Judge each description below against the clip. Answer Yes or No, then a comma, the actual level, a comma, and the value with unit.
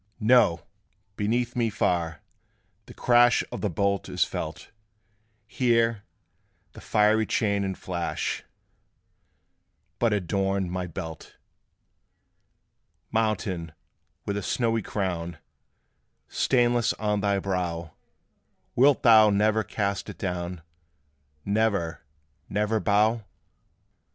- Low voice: Yes, low, 100 Hz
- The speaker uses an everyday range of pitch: Yes, average, 3.5 semitones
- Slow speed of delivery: Yes, slow, 95 wpm